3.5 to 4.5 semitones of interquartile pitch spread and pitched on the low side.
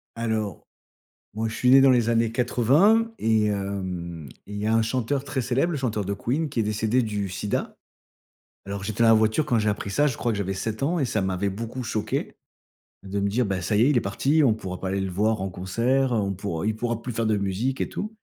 Yes: average, 3.8 semitones; low, 110 Hz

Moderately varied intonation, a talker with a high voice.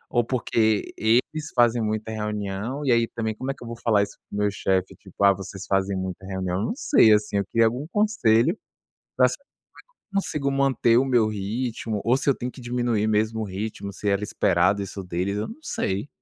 No: average, 3.6 semitones; low, 110 Hz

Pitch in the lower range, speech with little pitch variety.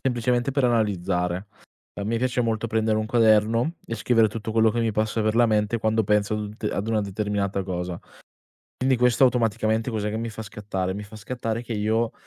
Yes: low, 110 Hz; narrow, 1.9 semitones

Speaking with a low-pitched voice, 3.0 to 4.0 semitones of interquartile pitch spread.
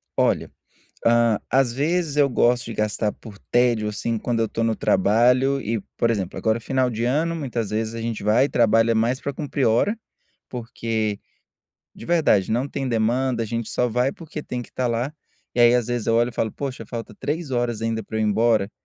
No: low, 120 Hz; narrow, 2.5 semitones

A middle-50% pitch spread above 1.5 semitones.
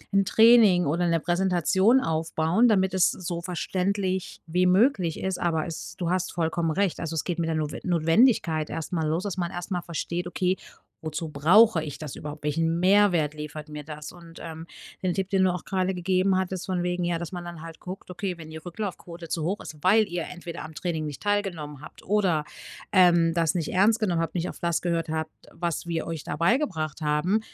Yes: narrow, 2.6 semitones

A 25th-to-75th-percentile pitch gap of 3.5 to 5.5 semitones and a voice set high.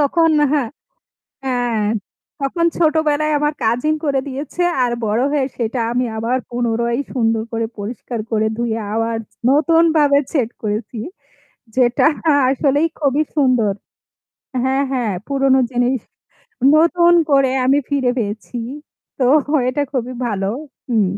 Yes: average, 3.9 semitones; very high, 255 Hz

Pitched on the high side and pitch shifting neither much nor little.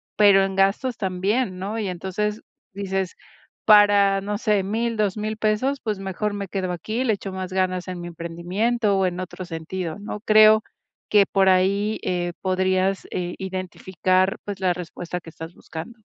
No: high, 195 Hz; narrow, 2.3 semitones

